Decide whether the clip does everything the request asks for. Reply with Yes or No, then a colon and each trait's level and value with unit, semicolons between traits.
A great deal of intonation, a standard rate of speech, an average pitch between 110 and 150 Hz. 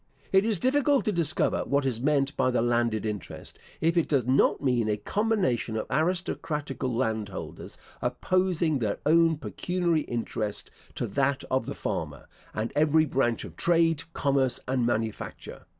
Yes: wide, 5.8 semitones; average, 150 wpm; medium, 140 Hz